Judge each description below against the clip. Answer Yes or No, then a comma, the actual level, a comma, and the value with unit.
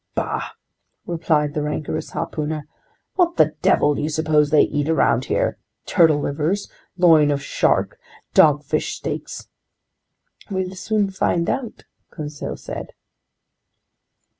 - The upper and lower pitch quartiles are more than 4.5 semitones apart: No, average, 2.9 semitones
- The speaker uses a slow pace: Yes, slow, 115 wpm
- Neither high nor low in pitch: Yes, medium, 155 Hz